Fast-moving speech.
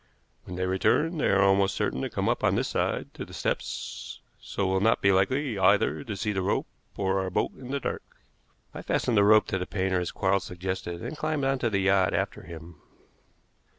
Yes: fast, 220 wpm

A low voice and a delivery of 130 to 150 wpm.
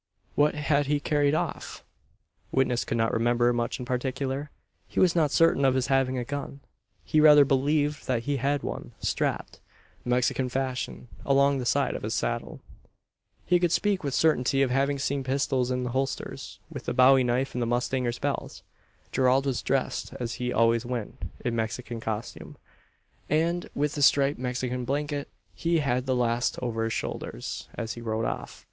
No: low, 130 Hz; average, 175 wpm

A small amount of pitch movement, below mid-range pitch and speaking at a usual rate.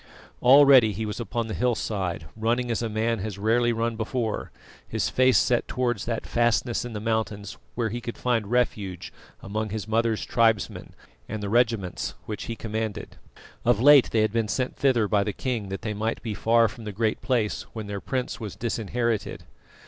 Yes: narrow, 2.1 semitones; low, 115 Hz; average, 185 wpm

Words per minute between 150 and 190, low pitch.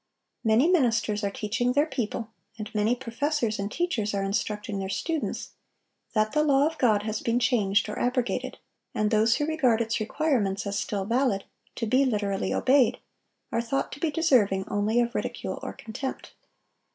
No: average, 170 wpm; high, 230 Hz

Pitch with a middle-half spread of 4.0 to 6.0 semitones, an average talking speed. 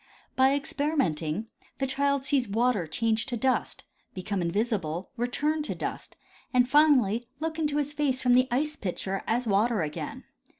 Yes: wide, 5.6 semitones; average, 155 wpm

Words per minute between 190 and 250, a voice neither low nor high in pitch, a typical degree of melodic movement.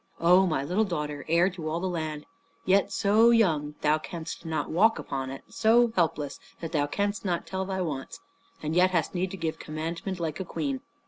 Yes: average, 200 wpm; medium, 170 Hz; average, 3.6 semitones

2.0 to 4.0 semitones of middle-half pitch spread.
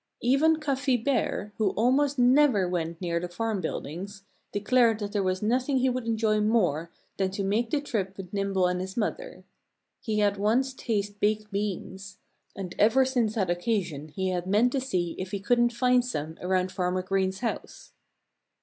No: average, 4.6 semitones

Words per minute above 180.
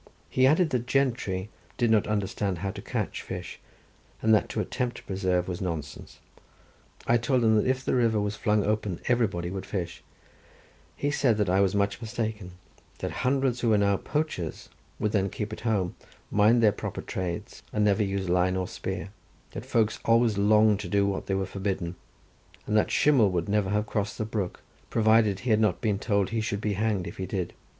Yes: average, 200 wpm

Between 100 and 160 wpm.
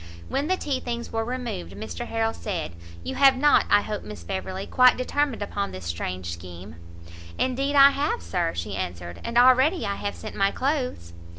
No: average, 185 wpm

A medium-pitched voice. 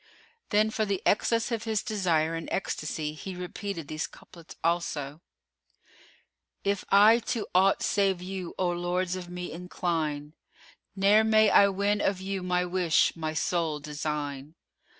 Yes: medium, 180 Hz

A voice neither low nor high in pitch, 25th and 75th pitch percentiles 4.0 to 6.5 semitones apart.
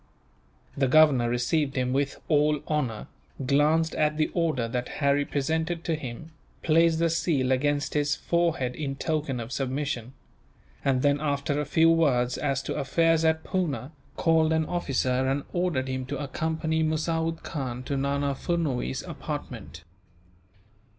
No: medium, 145 Hz; average, 3.3 semitones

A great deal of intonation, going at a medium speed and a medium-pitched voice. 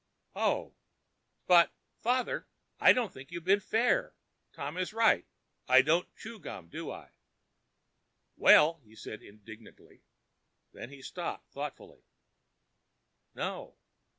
No: wide, 8.4 semitones; slow, 120 wpm; medium, 165 Hz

